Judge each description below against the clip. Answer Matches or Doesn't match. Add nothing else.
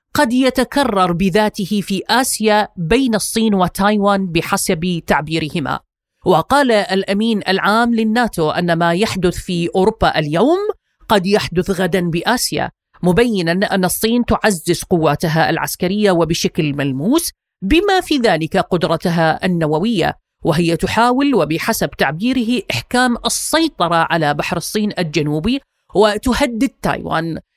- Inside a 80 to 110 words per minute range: Matches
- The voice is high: Matches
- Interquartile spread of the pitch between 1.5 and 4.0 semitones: Doesn't match